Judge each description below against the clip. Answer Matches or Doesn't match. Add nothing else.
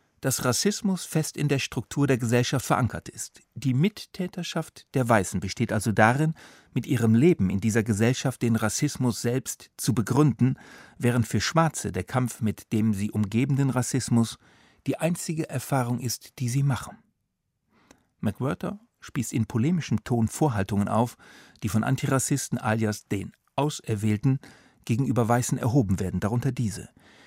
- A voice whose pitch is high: Doesn't match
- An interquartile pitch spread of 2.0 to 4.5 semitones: Matches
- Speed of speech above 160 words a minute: Doesn't match